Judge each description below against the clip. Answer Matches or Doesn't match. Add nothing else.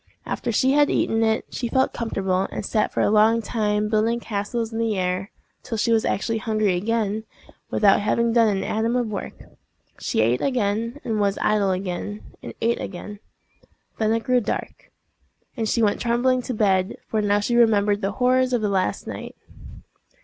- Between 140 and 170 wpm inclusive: Doesn't match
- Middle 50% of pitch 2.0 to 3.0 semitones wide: Matches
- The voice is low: Doesn't match